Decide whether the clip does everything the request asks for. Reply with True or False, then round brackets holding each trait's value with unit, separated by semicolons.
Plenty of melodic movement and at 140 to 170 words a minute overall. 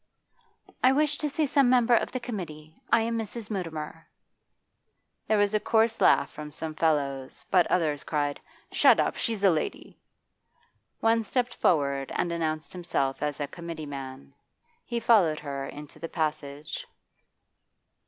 True (7.2 semitones; 150 wpm)